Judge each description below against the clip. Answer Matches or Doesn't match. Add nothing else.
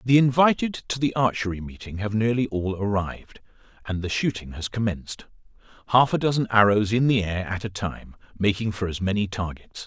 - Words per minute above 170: Matches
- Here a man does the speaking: Matches